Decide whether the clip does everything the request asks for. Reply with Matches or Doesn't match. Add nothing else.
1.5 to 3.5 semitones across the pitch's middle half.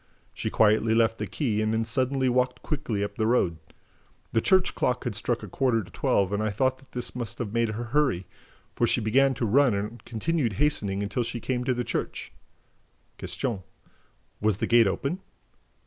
Matches